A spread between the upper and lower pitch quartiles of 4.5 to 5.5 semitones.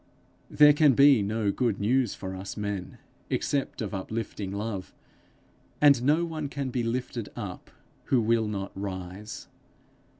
Yes: average, 5.0 semitones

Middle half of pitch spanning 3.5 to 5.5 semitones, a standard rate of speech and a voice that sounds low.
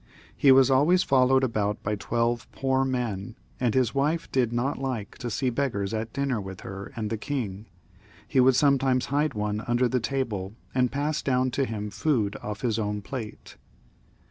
Yes: average, 4.0 semitones; average, 185 wpm; low, 125 Hz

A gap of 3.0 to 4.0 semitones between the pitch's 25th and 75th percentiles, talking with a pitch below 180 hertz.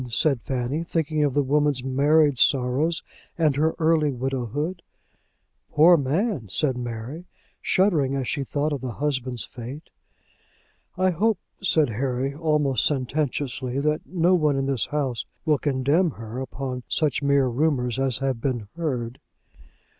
Yes: average, 3.3 semitones; medium, 140 Hz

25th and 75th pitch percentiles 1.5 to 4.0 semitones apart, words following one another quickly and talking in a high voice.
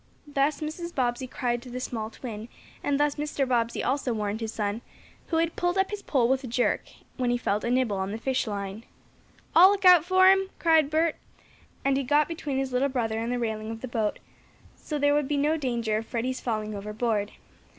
No: average, 4.7 semitones; fast, 215 wpm; very high, 255 Hz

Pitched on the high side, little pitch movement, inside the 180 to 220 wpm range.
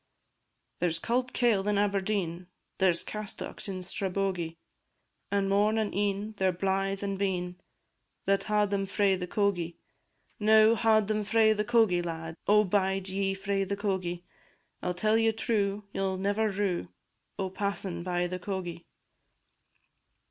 No: high, 195 Hz; narrow, 2.3 semitones; average, 155 wpm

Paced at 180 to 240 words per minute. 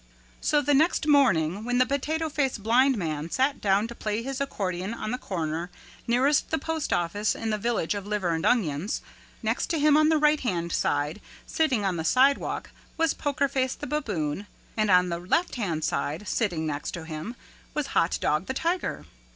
Yes: average, 190 wpm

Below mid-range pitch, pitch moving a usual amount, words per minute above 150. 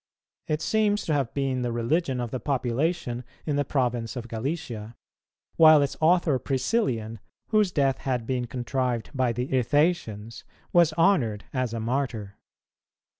No: low, 130 Hz; average, 4.6 semitones; average, 145 wpm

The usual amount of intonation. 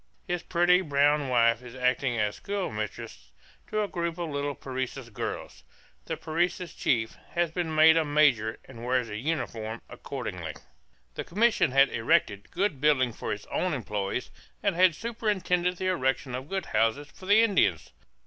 No: wide, 7.0 semitones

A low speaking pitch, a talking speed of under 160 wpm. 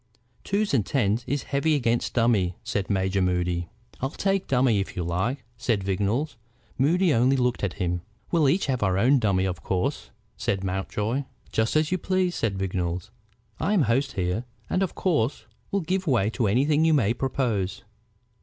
No: low, 115 Hz; average, 175 wpm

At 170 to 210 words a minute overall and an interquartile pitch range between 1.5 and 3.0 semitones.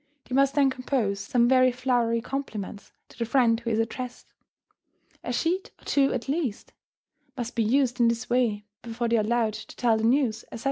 Yes: average, 195 wpm; narrow, 2.5 semitones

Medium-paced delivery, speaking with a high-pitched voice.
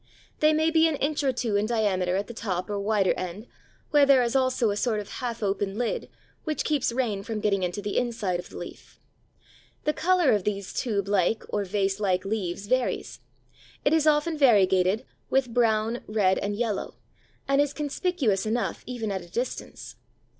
Yes: average, 190 wpm; high, 220 Hz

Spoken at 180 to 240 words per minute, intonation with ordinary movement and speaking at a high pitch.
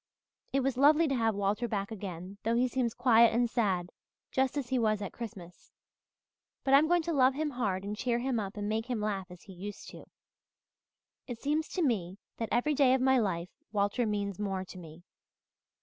Yes: average, 200 wpm; average, 4.6 semitones; high, 225 Hz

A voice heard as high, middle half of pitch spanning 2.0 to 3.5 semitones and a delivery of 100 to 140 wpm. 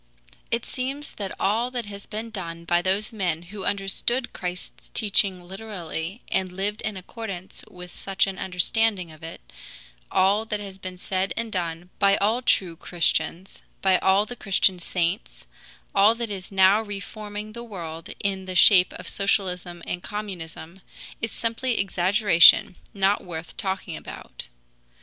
No: high, 195 Hz; average, 2.9 semitones; average, 150 wpm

